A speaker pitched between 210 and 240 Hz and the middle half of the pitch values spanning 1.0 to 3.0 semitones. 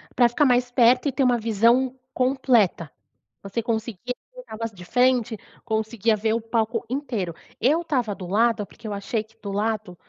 Yes: high, 230 Hz; average, 2.7 semitones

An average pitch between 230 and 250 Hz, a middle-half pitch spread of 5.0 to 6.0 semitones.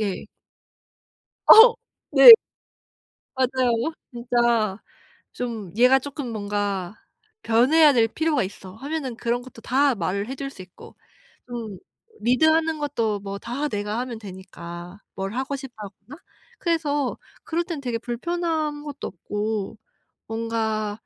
Yes: high, 240 Hz; average, 5.3 semitones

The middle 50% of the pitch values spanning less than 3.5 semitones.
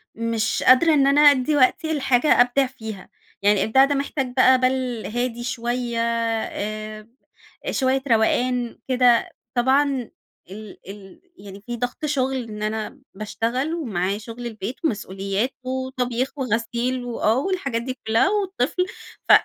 Yes: average, 3.1 semitones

